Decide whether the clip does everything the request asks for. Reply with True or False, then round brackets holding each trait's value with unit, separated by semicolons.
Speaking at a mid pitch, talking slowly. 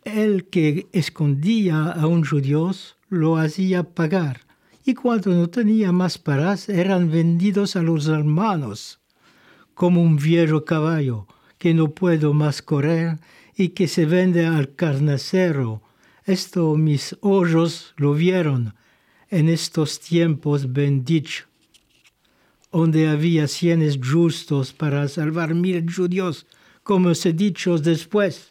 True (165 Hz; 120 wpm)